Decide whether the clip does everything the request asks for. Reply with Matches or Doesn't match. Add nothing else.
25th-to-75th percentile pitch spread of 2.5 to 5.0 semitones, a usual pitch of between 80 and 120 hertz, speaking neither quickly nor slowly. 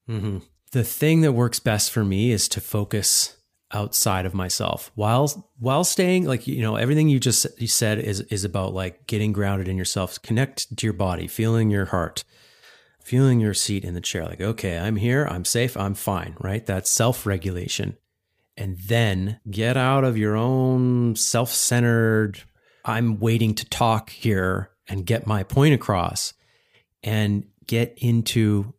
Matches